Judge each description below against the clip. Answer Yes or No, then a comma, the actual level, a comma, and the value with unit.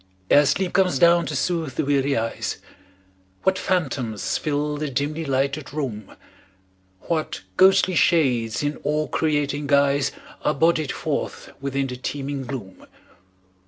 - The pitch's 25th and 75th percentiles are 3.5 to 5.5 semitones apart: No, average, 2.7 semitones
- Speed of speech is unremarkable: No, slow, 130 wpm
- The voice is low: No, medium, 145 Hz